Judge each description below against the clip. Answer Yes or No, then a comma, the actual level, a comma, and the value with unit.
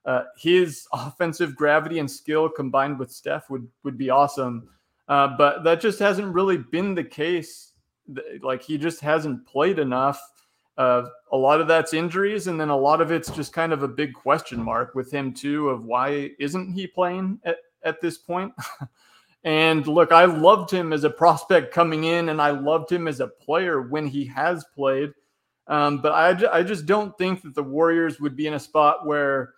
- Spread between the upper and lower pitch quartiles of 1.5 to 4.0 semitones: Yes, average, 3.3 semitones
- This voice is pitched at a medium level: Yes, medium, 155 Hz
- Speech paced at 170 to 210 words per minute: Yes, average, 195 wpm